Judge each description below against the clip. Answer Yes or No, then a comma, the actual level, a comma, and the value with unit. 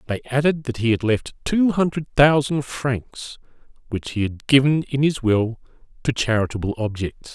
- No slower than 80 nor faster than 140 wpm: No, average, 165 wpm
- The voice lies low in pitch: Yes, low, 130 Hz